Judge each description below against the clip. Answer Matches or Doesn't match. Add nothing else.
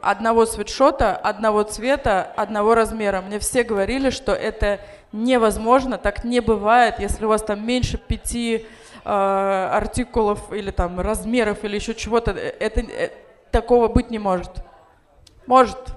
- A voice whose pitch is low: Doesn't match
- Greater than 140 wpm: Doesn't match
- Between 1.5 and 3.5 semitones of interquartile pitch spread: Matches